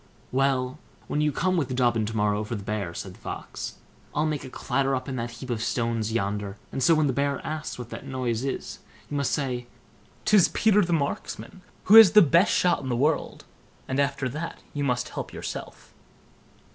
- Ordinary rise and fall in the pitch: Yes, average, 4.2 semitones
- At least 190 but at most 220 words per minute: Yes, fast, 205 wpm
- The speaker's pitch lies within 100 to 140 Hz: Yes, low, 135 Hz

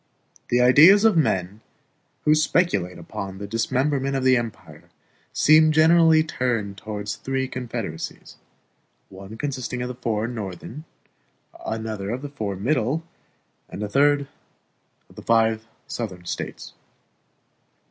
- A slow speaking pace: Yes, slow, 125 wpm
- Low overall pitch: Yes, low, 120 Hz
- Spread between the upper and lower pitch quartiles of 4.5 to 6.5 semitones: Yes, wide, 5.5 semitones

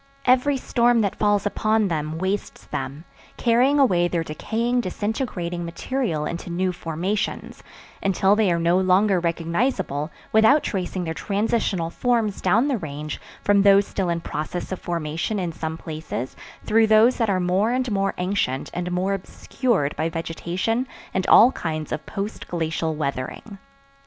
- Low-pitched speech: No, high, 190 Hz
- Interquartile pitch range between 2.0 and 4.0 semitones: No, average, 4.7 semitones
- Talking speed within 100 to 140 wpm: No, average, 150 wpm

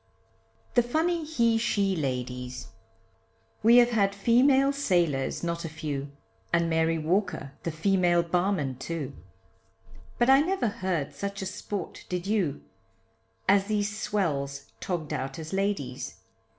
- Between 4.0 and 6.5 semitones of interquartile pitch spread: Yes, wide, 5.6 semitones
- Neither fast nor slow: No, slow, 130 wpm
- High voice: No, medium, 180 Hz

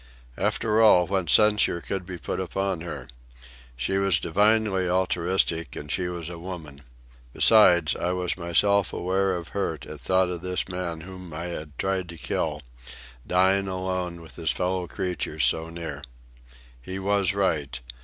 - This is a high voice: No, very low, 90 Hz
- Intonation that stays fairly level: Yes, narrow, 2.2 semitones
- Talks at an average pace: Yes, average, 155 wpm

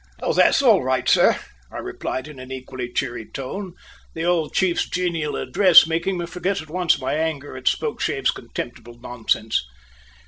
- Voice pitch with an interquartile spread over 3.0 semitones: Yes, average, 5.2 semitones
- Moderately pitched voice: Yes, medium, 155 Hz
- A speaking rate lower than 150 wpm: No, average, 165 wpm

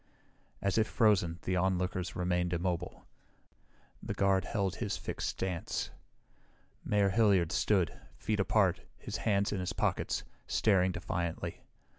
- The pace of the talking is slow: Yes, slow, 125 wpm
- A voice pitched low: Yes, very low, 95 Hz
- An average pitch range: No, narrow, 2.2 semitones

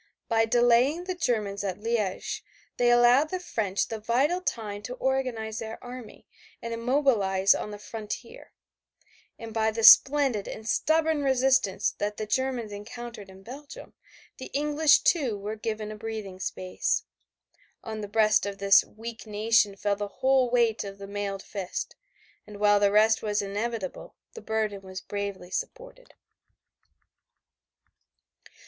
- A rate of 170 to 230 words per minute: No, average, 145 wpm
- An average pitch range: Yes, average, 3.7 semitones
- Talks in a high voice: Yes, high, 220 Hz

